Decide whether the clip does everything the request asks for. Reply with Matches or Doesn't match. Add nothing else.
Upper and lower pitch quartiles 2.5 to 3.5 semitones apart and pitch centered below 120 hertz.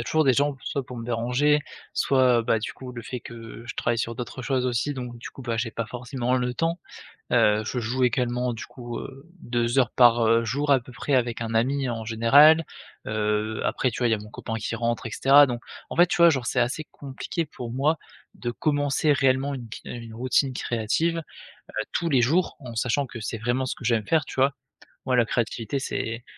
Doesn't match